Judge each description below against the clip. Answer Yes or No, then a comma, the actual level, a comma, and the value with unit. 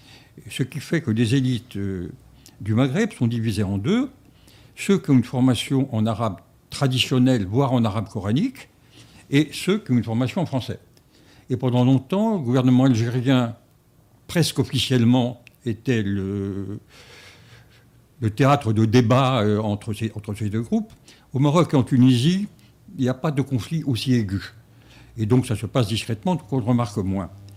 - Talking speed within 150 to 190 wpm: Yes, average, 160 wpm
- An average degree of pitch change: Yes, average, 3.4 semitones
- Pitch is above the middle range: No, low, 125 Hz